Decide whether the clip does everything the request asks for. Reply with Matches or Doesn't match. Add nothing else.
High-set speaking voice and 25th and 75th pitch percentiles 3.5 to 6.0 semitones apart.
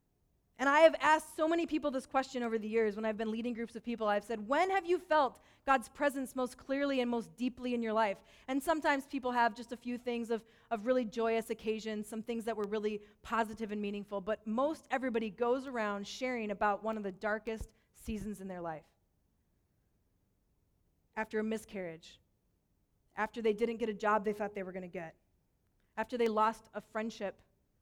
Doesn't match